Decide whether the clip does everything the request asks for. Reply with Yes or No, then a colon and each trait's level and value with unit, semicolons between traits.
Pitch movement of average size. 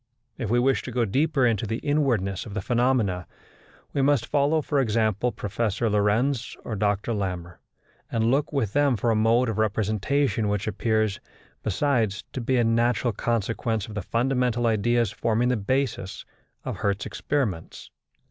Yes: average, 3.4 semitones